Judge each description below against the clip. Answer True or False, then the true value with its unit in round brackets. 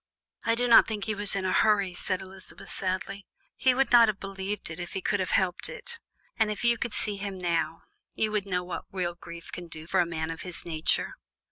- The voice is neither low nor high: False (195 Hz)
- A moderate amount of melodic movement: True (3.2 semitones)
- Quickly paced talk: True (235 wpm)